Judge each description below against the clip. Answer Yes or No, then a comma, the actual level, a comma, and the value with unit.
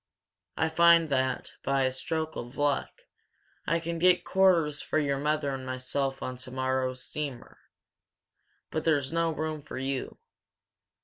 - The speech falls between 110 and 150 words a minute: Yes, average, 140 wpm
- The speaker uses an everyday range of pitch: Yes, average, 3.5 semitones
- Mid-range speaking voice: Yes, medium, 145 Hz